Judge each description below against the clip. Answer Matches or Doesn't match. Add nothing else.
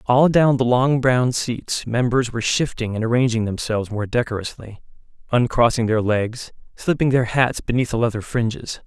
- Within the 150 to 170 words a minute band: Matches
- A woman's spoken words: Doesn't match